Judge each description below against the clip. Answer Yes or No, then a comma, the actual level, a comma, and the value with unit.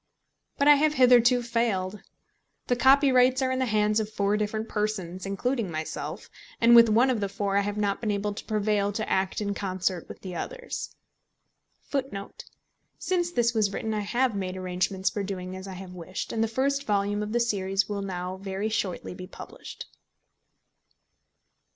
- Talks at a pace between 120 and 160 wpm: No, average, 180 wpm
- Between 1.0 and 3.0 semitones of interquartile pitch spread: No, average, 3.6 semitones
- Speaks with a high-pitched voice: Yes, high, 210 Hz